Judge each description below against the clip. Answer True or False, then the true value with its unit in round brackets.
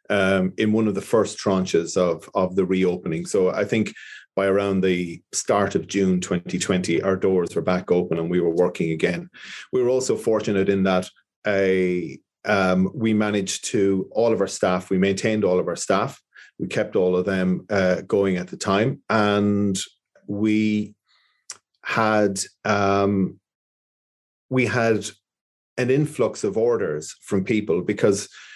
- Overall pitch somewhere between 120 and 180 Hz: False (100 Hz)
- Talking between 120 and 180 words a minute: True (160 wpm)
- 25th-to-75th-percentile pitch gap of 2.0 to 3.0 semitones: True (2.7 semitones)